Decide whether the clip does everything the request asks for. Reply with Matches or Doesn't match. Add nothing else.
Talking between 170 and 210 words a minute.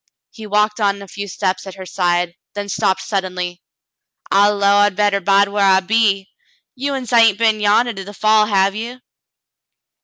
Matches